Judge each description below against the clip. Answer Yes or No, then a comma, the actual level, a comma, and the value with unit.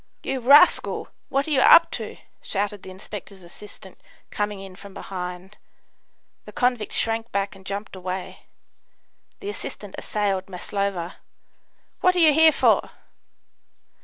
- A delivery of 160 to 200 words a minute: No, slow, 135 wpm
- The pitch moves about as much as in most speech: Yes, average, 4.7 semitones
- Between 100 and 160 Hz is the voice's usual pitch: No, high, 200 Hz